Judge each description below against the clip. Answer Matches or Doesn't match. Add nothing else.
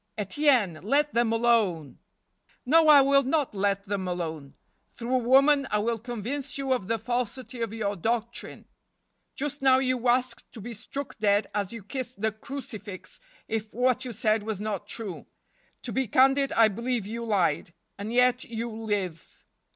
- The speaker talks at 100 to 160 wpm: Doesn't match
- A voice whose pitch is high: Matches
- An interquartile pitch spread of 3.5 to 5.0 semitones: Matches